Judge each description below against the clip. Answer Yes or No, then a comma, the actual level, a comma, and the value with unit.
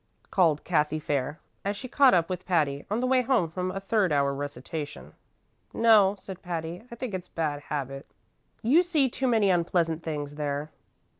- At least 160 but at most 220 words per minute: Yes, average, 180 wpm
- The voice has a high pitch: No, medium, 175 Hz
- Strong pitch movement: Yes, wide, 6.0 semitones